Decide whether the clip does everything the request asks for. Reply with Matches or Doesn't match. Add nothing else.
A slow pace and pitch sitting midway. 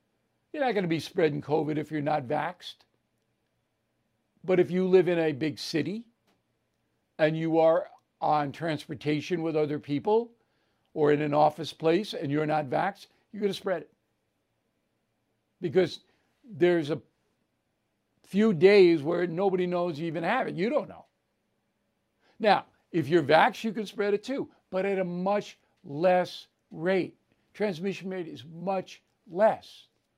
Doesn't match